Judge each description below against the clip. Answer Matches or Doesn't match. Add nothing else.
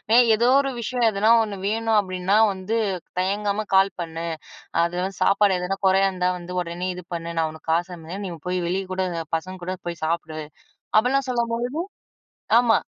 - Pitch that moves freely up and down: Doesn't match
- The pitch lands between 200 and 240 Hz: Doesn't match